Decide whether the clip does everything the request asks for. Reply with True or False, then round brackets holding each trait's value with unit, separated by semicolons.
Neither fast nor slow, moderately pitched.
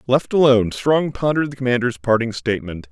False (165 wpm; 125 Hz)